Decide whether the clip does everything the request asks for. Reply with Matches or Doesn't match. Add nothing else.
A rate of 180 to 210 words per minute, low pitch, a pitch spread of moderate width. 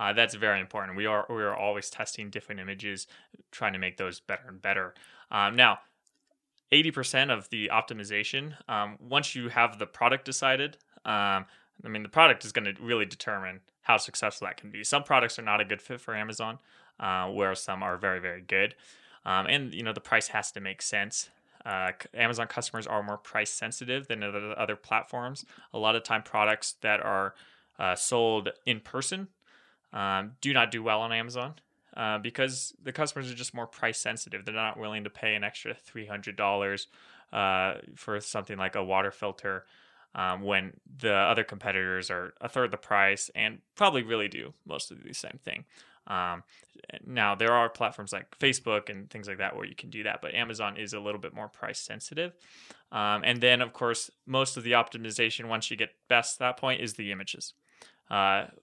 Matches